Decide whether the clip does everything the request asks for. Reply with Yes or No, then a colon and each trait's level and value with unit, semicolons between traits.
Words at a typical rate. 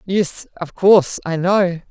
Yes: average, 155 wpm